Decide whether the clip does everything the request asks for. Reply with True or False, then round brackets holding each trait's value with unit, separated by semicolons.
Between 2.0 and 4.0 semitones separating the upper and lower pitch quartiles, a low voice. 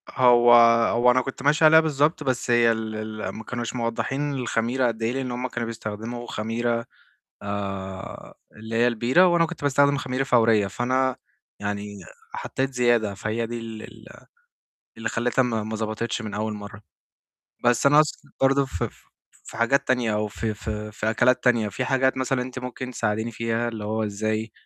True (2.9 semitones; 120 Hz)